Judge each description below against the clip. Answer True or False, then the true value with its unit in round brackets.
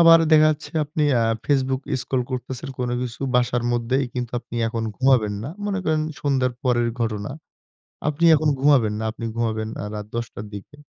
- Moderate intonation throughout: True (3.8 semitones)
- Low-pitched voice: True (125 Hz)